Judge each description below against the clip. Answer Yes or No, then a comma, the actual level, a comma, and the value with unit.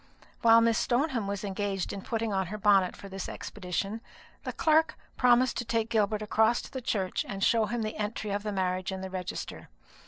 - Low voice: No, high, 210 Hz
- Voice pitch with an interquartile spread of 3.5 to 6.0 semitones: No, average, 2.9 semitones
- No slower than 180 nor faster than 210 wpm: Yes, average, 200 wpm